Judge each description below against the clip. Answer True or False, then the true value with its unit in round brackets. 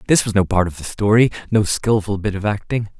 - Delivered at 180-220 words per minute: False (240 wpm)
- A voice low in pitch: True (105 Hz)